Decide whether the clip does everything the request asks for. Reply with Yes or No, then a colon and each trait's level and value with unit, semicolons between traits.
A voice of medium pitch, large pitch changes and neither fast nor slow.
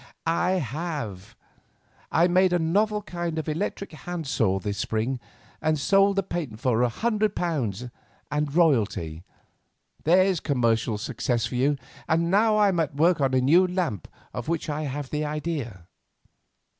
Yes: medium, 155 Hz; wide, 6.2 semitones; average, 155 wpm